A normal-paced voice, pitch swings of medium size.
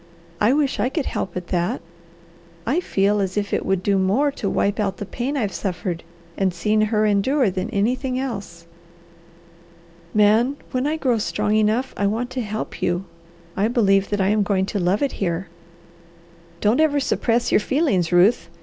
Yes: average, 180 wpm; average, 4.5 semitones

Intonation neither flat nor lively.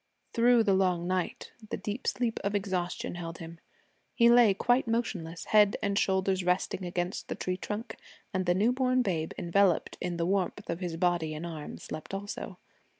Yes: average, 3.1 semitones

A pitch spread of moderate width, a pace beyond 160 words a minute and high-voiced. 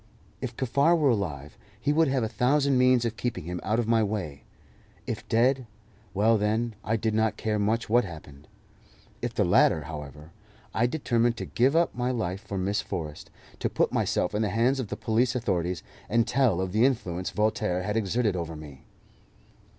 No: average, 4.9 semitones; average, 190 wpm; low, 110 Hz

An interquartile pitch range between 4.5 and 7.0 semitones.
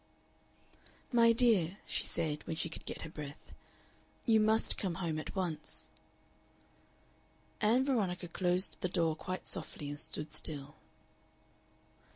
Yes: average, 5.3 semitones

